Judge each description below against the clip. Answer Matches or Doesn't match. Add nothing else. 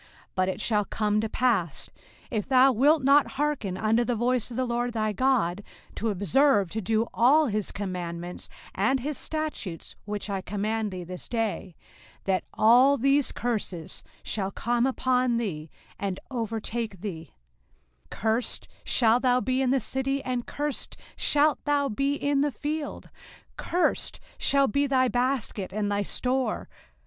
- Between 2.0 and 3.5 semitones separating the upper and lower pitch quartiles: Doesn't match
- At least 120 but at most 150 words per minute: Doesn't match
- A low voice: Doesn't match